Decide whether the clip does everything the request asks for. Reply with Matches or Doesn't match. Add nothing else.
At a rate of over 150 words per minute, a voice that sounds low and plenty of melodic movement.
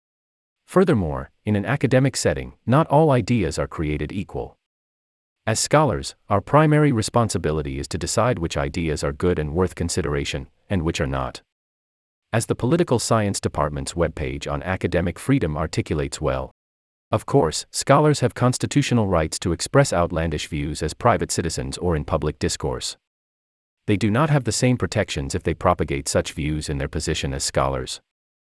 Matches